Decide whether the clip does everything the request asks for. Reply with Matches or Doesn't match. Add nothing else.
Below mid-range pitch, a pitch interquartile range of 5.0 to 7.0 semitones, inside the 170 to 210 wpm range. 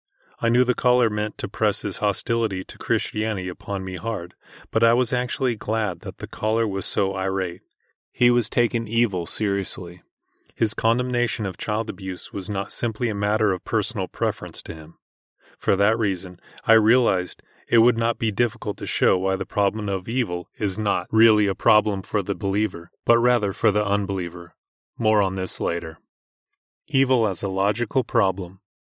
Doesn't match